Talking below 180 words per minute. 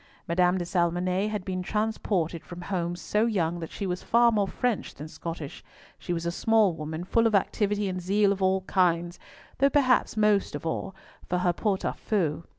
No: average, 195 wpm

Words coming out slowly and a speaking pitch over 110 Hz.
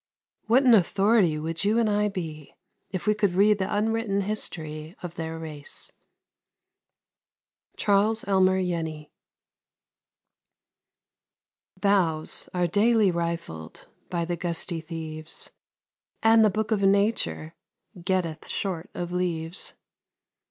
Yes: slow, 110 wpm; medium, 185 Hz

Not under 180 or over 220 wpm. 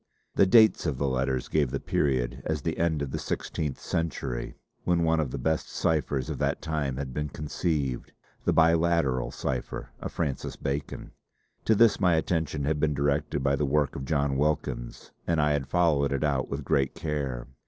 Yes: average, 185 wpm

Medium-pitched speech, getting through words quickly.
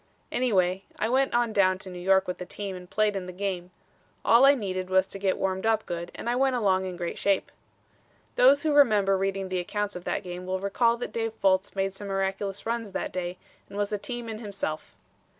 No: high, 195 Hz; fast, 225 wpm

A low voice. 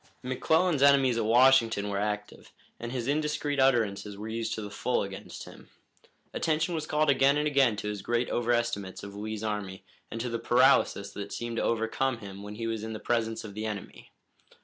Yes: low, 115 Hz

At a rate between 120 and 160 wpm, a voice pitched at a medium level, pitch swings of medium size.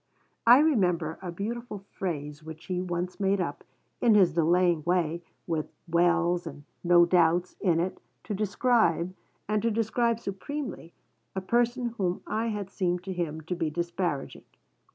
Yes: average, 155 wpm; medium, 180 Hz; average, 3.6 semitones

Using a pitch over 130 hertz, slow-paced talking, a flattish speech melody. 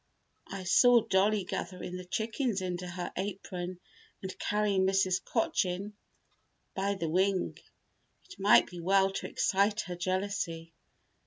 Yes: high, 190 Hz; slow, 130 wpm; narrow, 1.8 semitones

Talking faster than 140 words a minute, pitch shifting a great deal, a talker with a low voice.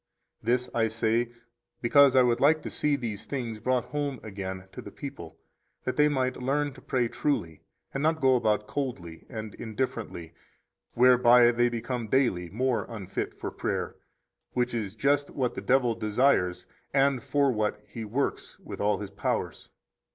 No: average, 165 wpm; average, 3.6 semitones; low, 120 Hz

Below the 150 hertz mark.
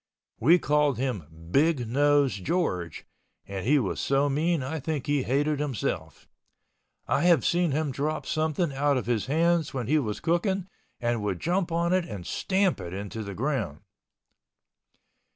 Yes: medium, 140 Hz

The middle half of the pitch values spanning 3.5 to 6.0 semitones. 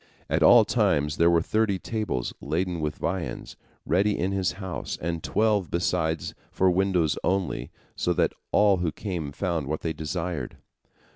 No: average, 3.1 semitones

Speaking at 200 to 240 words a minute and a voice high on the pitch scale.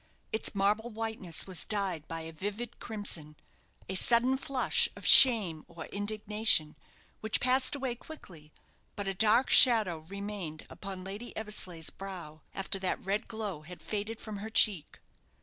No: average, 150 wpm; high, 205 Hz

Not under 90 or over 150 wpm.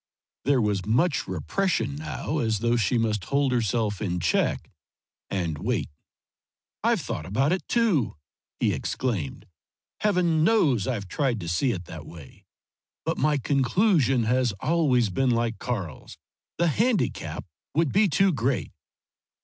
Yes: average, 140 wpm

